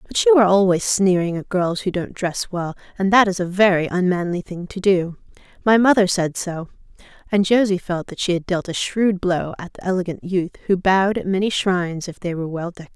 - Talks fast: Yes, fast, 225 wpm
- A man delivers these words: No, female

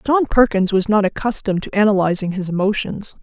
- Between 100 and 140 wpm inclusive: No, average, 170 wpm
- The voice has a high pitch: Yes, high, 205 Hz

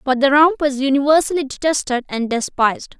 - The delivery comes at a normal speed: Yes, average, 160 wpm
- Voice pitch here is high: Yes, very high, 275 Hz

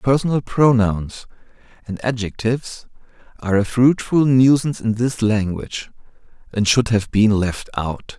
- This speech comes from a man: Yes, male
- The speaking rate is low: Yes, slow, 125 wpm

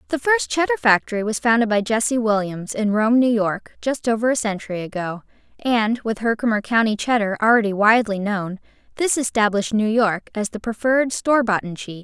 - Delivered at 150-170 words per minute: No, average, 180 wpm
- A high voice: Yes, high, 220 Hz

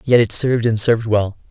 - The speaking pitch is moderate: No, low, 115 Hz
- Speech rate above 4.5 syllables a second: Yes, 6.2 syllables/s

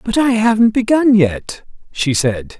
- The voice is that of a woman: No, male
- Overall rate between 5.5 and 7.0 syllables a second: No, 4.0 syllables/s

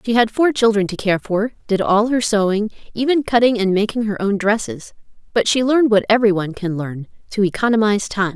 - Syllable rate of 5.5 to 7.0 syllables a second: Yes, 6.0 syllables/s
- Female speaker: Yes, female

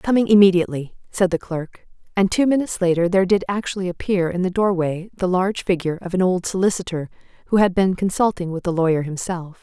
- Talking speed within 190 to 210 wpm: Yes, average, 195 wpm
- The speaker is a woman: Yes, female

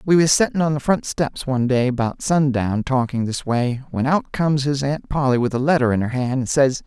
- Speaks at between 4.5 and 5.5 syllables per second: Yes, 5.4 syllables/s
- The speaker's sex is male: Yes, male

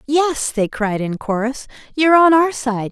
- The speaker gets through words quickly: No, average, 185 wpm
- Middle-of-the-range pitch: No, very high, 260 Hz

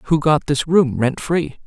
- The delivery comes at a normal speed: No, fast, 215 wpm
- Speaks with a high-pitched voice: No, medium, 150 Hz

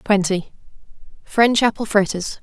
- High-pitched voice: Yes, high, 205 Hz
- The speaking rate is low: Yes, slow, 75 wpm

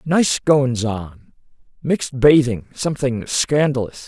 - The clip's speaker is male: Yes, male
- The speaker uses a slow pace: Yes, slow, 90 wpm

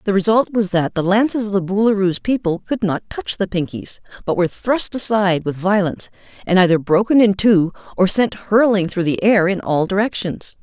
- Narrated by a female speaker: Yes, female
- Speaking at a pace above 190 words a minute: Yes, average, 200 wpm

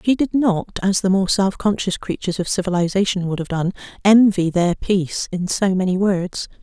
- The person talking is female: Yes, female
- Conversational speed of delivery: Yes, average, 190 wpm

